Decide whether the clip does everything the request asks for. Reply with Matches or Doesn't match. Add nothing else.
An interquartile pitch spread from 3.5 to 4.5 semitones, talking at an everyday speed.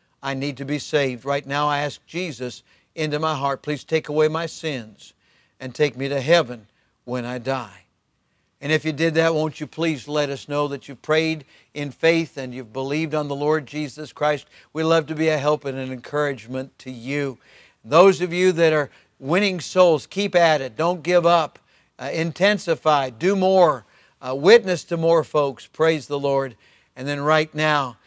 Doesn't match